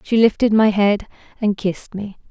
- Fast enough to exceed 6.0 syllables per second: No, 5.1 syllables/s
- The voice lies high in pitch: Yes, high, 205 Hz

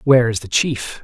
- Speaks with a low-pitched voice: Yes, low, 120 Hz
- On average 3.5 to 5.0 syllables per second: No, 5.4 syllables/s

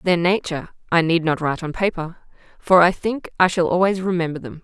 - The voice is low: No, medium, 170 Hz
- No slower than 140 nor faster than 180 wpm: No, fast, 205 wpm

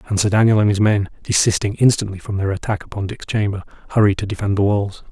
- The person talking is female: No, male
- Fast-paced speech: Yes, fast, 225 wpm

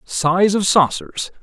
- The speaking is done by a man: Yes, male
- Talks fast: No, slow, 125 wpm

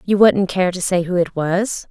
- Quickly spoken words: Yes, fast, 250 wpm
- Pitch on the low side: No, medium, 185 Hz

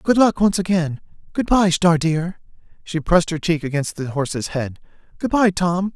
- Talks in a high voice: No, medium, 170 Hz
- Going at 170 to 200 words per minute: Yes, average, 190 wpm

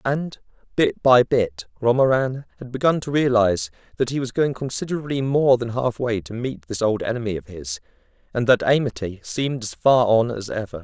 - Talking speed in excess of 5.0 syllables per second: Yes, 5.3 syllables/s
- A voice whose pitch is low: Yes, low, 120 Hz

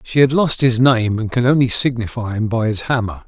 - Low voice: Yes, low, 120 Hz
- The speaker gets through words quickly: Yes, fast, 240 wpm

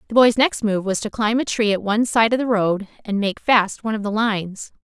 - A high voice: Yes, high, 215 Hz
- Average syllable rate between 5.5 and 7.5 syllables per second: Yes, 5.7 syllables/s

